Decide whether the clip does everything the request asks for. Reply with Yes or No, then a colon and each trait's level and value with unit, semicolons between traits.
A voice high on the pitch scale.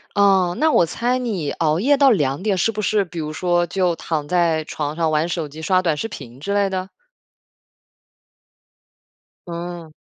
No: medium, 175 Hz